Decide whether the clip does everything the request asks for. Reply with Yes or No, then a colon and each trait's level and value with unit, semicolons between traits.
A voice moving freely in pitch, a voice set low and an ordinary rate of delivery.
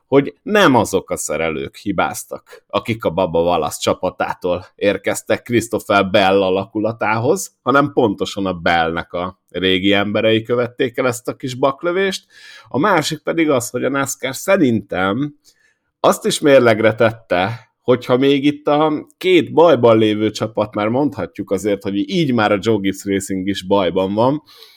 Yes: wide, 6.3 semitones; low, 120 Hz; average, 145 wpm